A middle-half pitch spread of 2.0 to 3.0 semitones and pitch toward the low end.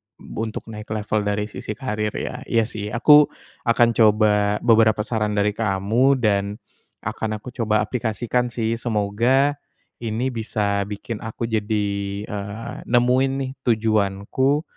Yes: narrow, 2.4 semitones; low, 110 Hz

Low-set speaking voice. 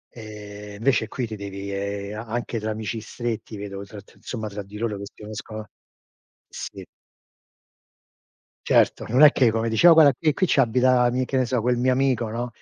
Yes: low, 110 Hz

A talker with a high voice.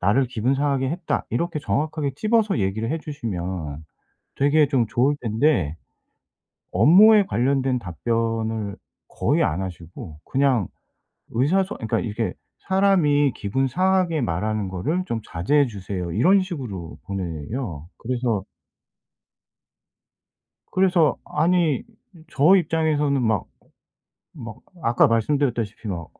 No: low, 125 Hz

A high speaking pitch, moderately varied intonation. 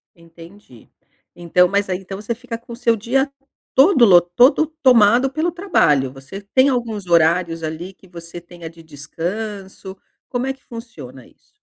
No: high, 195 Hz; wide, 6.1 semitones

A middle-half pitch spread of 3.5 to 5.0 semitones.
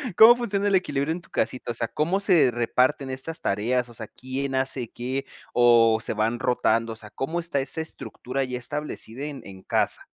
Yes: average, 4.3 semitones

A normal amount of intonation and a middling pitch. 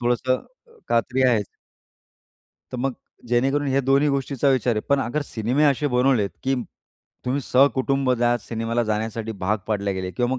No: average, 3.3 semitones; low, 125 Hz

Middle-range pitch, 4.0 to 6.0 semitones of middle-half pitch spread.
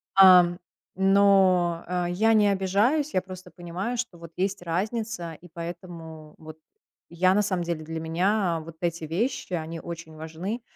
No: medium, 180 Hz; average, 2.8 semitones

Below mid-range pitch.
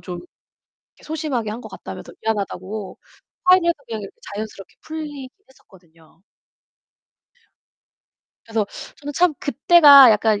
No: high, 230 Hz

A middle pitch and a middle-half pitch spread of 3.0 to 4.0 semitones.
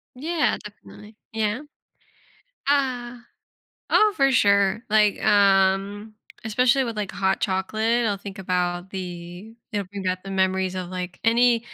No: high, 205 Hz; average, 3.3 semitones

